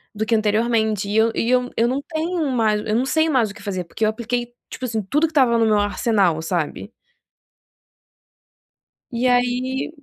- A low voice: No, high, 230 Hz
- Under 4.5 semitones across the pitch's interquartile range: Yes, average, 3.0 semitones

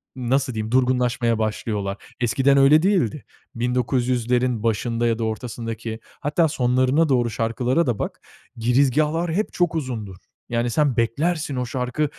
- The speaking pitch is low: Yes, low, 125 Hz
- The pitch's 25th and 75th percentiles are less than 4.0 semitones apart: Yes, average, 3.3 semitones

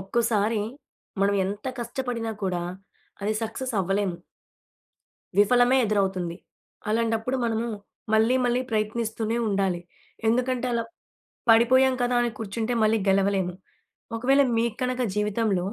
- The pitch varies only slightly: No, average, 3.0 semitones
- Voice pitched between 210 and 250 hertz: Yes, high, 225 Hz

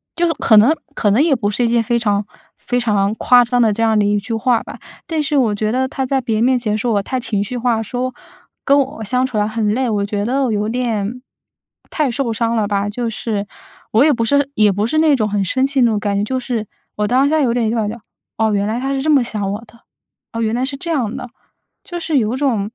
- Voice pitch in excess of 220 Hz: Yes, high, 230 Hz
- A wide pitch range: No, average, 3.5 semitones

